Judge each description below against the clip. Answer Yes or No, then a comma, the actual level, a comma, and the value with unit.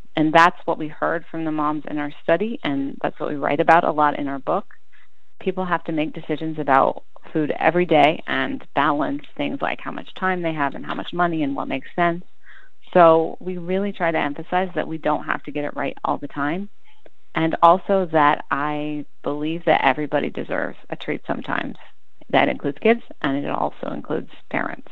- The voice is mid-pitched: Yes, medium, 160 Hz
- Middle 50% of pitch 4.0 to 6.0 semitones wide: No, average, 3.3 semitones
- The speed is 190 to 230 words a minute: Yes, average, 200 wpm